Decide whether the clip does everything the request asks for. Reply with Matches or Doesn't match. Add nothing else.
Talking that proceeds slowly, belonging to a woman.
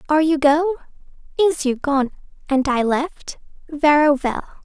Matches